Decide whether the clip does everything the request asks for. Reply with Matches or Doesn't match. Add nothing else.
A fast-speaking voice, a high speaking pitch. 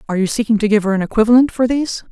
Matches